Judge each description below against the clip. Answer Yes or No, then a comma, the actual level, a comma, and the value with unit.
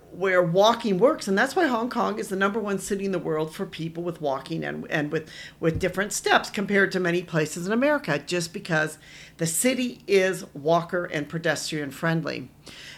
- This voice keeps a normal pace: Yes, average, 190 wpm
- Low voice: No, medium, 175 Hz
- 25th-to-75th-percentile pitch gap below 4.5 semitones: Yes, average, 4.1 semitones